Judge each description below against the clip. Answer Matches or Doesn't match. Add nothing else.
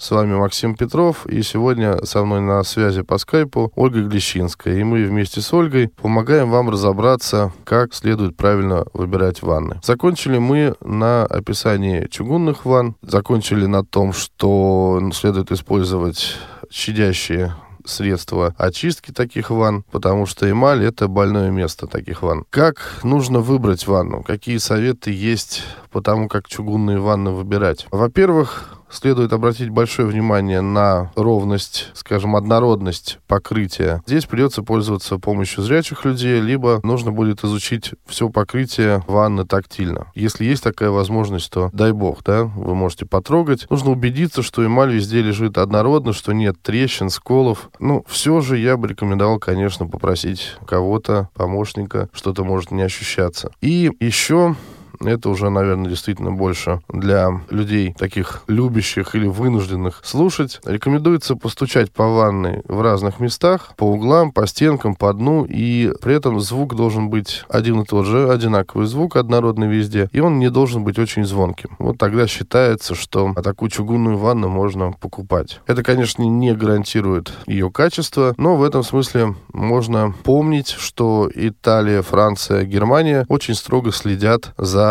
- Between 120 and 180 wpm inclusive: Matches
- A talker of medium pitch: Doesn't match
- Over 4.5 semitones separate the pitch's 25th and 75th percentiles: Doesn't match